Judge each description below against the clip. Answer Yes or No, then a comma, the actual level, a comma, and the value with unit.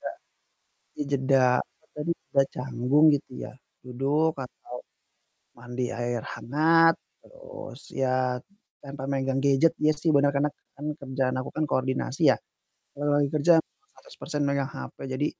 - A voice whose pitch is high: No, medium, 140 Hz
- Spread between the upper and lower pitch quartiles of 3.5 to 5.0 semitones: No, narrow, 2.6 semitones